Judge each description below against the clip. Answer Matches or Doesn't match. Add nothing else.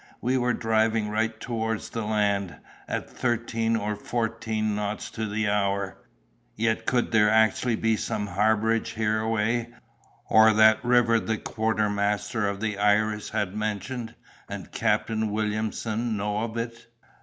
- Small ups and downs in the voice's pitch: Matches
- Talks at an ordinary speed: Doesn't match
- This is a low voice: Matches